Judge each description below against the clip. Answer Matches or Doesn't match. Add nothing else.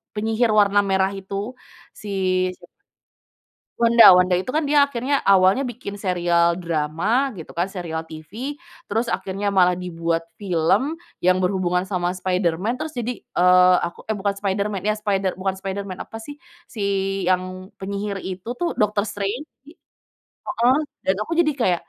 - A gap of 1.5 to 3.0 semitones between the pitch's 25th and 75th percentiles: Doesn't match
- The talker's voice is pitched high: Matches